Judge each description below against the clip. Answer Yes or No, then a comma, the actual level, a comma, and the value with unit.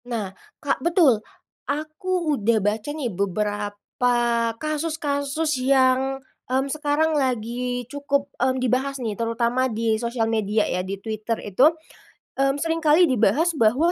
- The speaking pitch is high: Yes, very high, 255 Hz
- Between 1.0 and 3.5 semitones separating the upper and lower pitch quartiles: No, average, 4.6 semitones